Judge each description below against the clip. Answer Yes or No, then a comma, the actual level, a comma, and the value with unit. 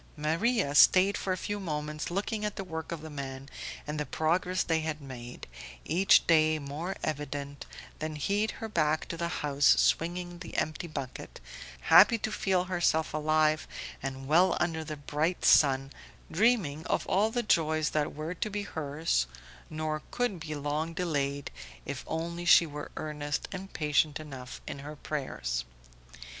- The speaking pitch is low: No, medium, 155 Hz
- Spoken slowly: No, average, 160 wpm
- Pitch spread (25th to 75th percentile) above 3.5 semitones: No, average, 3.2 semitones